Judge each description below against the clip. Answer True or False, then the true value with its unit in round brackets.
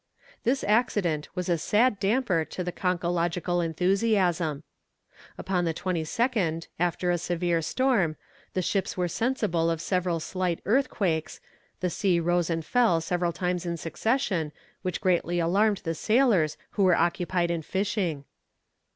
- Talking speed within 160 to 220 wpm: False (135 wpm)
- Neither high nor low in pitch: True (180 Hz)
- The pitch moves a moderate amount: True (3.1 semitones)